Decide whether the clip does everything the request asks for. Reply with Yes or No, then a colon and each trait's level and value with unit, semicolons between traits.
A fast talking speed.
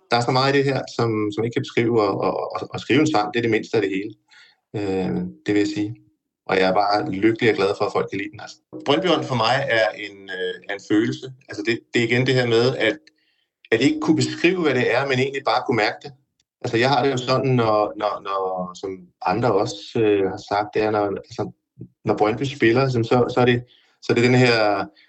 Yes: fast, 255 wpm